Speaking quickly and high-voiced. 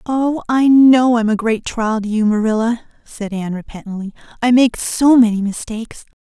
No: average, 175 wpm; high, 230 Hz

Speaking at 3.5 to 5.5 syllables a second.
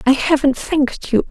Yes: 5.1 syllables/s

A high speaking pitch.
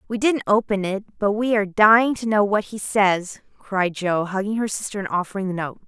Yes: high, 205 Hz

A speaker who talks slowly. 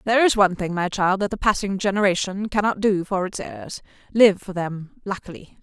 No: average, 180 wpm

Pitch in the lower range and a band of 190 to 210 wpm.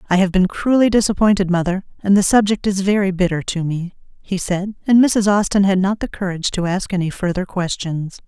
No: high, 190 Hz; fast, 205 wpm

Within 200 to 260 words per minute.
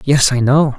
Yes: fast, 230 wpm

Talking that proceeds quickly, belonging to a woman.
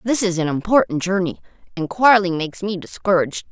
No: average, 170 wpm; female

